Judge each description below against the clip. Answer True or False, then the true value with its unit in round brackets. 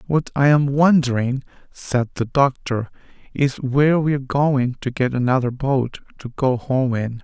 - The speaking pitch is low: True (130 Hz)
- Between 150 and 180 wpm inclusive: True (165 wpm)